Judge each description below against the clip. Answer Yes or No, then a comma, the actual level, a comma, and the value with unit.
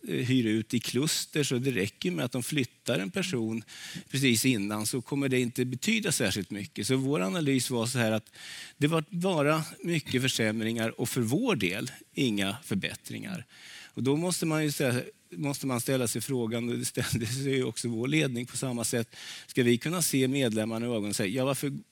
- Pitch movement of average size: Yes, average, 3.4 semitones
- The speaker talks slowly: No, fast, 195 wpm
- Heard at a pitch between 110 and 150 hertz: Yes, low, 130 Hz